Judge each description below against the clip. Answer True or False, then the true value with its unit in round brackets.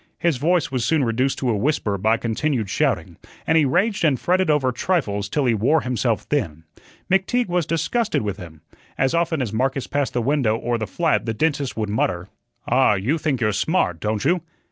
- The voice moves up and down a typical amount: False (6.5 semitones)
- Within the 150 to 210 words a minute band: True (200 wpm)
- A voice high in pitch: False (130 Hz)